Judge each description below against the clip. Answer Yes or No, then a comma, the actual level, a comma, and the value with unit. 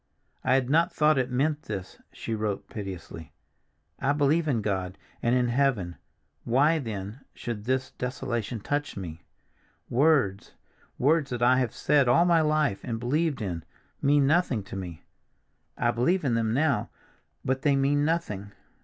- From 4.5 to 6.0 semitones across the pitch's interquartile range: Yes, wide, 5.4 semitones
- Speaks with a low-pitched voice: Yes, low, 125 Hz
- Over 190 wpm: No, average, 155 wpm